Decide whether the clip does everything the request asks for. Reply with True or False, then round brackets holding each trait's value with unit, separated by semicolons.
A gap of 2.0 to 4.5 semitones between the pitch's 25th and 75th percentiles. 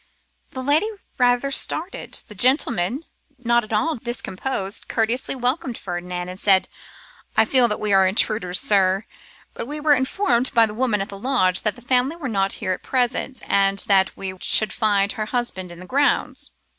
False (4.9 semitones)